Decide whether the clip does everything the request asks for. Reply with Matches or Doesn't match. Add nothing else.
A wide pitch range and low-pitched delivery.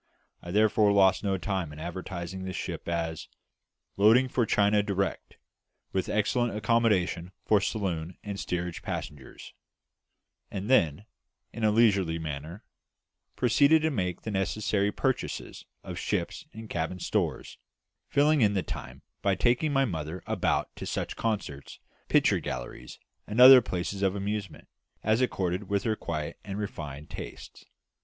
Doesn't match